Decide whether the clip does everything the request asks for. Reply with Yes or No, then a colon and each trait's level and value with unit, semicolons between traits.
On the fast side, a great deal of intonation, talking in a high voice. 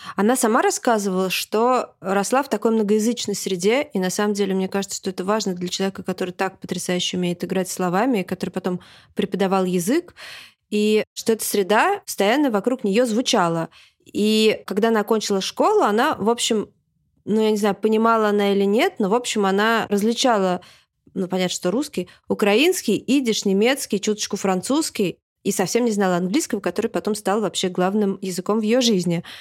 No: fast, 165 wpm; average, 3.1 semitones; high, 205 Hz